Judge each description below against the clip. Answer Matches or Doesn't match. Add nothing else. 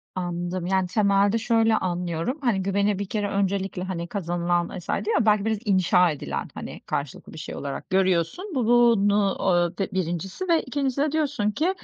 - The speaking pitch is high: Matches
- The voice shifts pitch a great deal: Doesn't match